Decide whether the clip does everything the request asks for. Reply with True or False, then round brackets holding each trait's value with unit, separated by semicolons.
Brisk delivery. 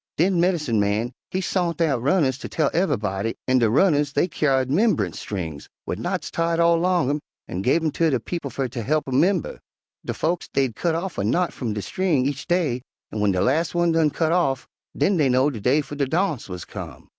True (225 wpm)